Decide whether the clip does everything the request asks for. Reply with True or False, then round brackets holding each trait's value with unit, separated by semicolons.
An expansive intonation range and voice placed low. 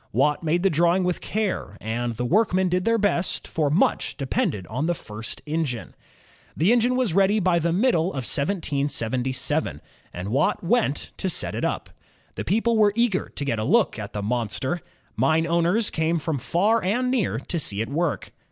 False (6.8 semitones; 165 Hz)